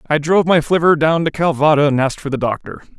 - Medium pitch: Yes, medium, 150 Hz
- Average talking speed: No, fast, 240 wpm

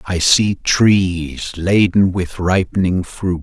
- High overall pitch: No, very low, 90 Hz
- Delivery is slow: Yes, slow, 125 wpm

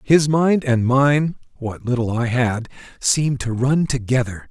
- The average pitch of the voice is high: No, low, 130 Hz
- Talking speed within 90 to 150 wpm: Yes, slow, 135 wpm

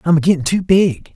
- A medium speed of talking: No, fast, 260 wpm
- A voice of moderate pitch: Yes, medium, 165 Hz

